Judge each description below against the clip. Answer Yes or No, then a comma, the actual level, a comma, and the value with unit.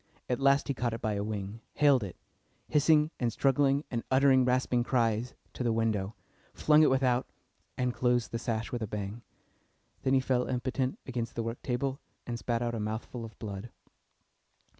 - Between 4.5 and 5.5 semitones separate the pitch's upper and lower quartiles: No, narrow, 2.6 semitones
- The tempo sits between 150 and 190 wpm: Yes, average, 180 wpm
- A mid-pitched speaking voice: No, low, 120 Hz